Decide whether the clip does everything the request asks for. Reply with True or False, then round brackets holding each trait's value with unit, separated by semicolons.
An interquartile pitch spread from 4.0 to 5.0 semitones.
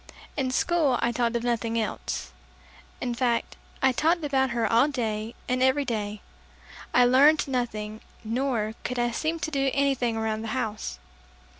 False (3.2 semitones)